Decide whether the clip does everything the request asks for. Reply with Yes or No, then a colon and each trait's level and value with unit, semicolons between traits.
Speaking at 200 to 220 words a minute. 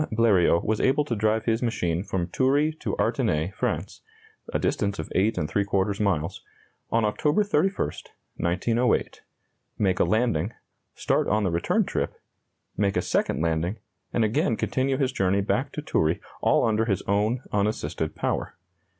No: average, 150 wpm